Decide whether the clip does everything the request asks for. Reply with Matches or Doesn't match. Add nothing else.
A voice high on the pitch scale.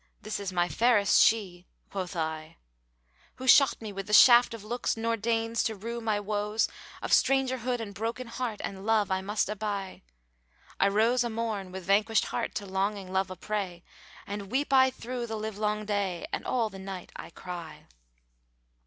Matches